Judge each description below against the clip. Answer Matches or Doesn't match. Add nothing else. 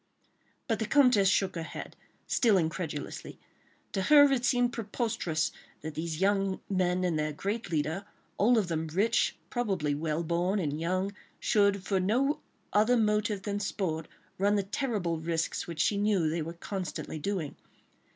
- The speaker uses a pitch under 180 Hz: Doesn't match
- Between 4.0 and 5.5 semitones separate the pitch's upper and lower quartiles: Matches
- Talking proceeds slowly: Doesn't match